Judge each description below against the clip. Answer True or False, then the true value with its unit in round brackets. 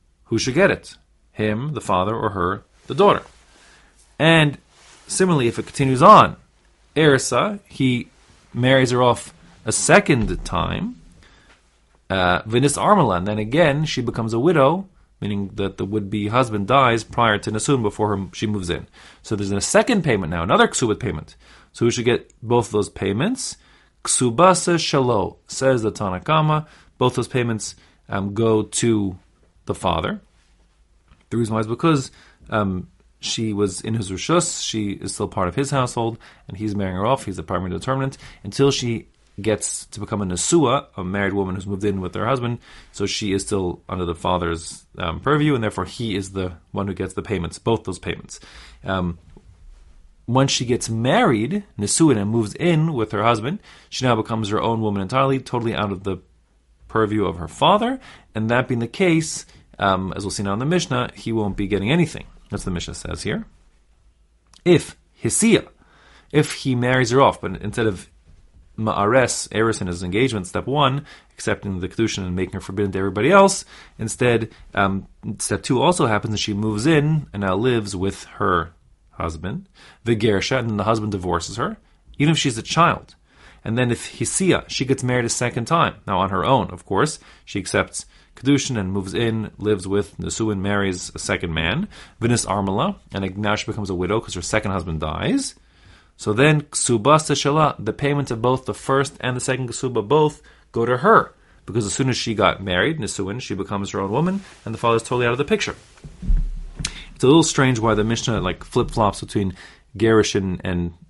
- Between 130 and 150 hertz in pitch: False (110 Hz)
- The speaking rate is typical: True (185 wpm)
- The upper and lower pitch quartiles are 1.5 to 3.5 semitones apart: False (5.3 semitones)